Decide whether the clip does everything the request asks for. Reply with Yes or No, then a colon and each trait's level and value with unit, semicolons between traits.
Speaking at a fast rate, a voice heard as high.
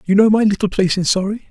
Yes: fast, 280 wpm; high, 200 Hz